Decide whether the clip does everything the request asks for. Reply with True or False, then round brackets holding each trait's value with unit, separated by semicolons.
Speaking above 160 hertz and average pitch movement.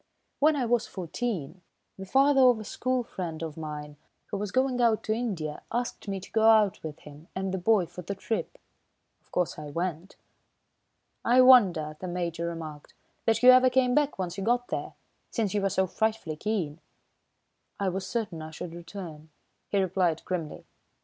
False (190 Hz; 5.7 semitones)